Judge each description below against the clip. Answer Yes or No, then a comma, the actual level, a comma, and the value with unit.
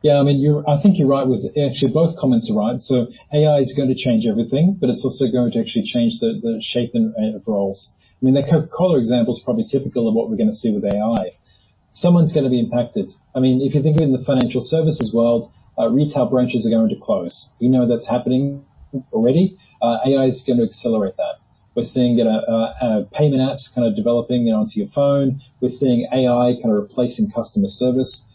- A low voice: Yes, low, 130 Hz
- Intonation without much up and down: No, average, 4.1 semitones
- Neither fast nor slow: No, fast, 235 wpm